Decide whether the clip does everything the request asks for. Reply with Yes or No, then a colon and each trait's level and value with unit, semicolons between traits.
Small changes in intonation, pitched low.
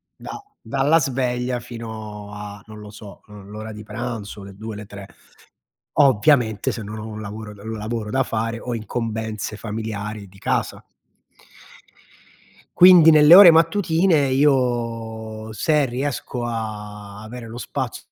No: average, 3.2 semitones; low, 110 Hz